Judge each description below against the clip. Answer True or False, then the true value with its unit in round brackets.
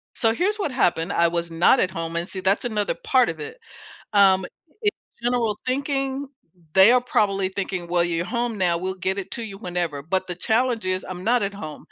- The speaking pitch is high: True (195 Hz)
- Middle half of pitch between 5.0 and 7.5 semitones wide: True (5.3 semitones)